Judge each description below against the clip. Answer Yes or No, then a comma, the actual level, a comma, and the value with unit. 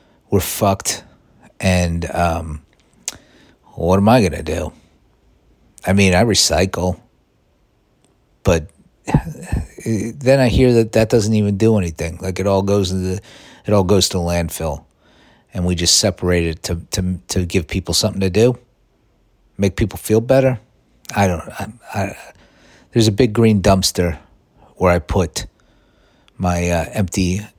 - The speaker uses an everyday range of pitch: Yes, average, 4.0 semitones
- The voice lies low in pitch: Yes, very low, 95 Hz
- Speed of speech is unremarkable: Yes, average, 145 wpm